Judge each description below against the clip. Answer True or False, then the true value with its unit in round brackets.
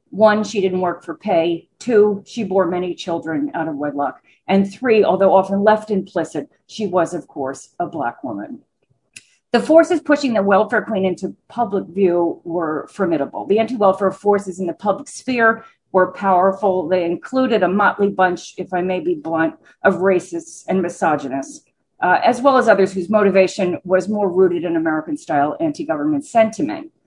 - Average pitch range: True (3.9 semitones)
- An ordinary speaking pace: True (175 wpm)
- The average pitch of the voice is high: True (195 Hz)